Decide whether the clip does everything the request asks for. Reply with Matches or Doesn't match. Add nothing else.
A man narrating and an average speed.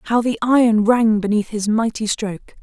Doesn't match